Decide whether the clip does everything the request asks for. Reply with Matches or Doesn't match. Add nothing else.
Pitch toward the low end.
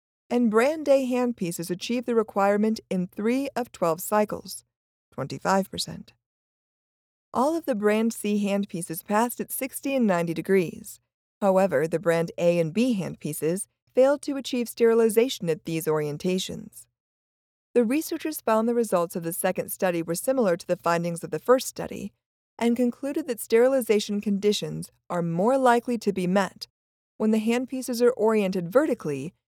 Doesn't match